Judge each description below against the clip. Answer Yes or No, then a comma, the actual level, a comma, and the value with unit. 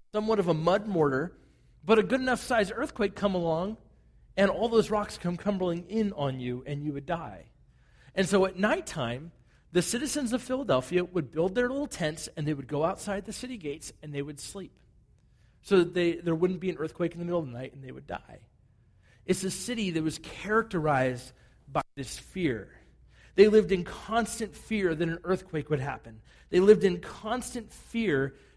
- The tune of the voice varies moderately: No, wide, 6.7 semitones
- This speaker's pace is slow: No, average, 195 wpm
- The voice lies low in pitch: No, medium, 175 Hz